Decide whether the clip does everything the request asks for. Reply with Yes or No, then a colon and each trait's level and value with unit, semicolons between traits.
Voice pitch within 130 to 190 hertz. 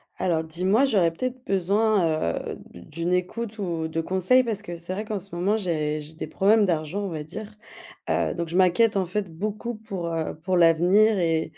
Yes: medium, 185 Hz